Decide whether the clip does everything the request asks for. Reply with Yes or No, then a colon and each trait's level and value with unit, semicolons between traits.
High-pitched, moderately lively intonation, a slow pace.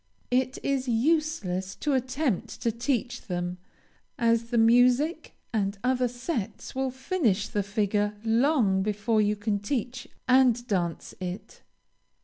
Yes: high, 230 Hz; average, 3.9 semitones; slow, 130 wpm